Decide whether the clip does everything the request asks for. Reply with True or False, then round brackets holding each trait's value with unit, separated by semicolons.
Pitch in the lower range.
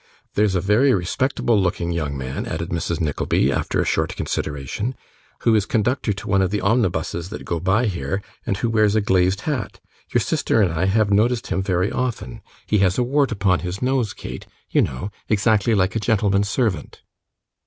True (100 Hz)